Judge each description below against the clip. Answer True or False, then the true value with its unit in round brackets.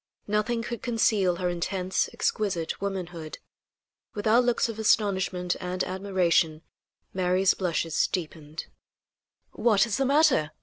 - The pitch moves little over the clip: False (3.5 semitones)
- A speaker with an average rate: False (120 wpm)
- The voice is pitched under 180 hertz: False (190 Hz)